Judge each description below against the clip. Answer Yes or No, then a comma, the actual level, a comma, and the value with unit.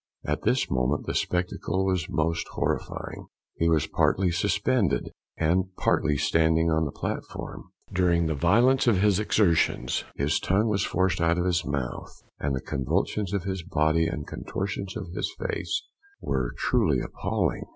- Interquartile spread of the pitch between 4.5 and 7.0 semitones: No, average, 3.4 semitones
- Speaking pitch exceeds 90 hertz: No, very low, 85 Hz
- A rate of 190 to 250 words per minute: No, average, 155 wpm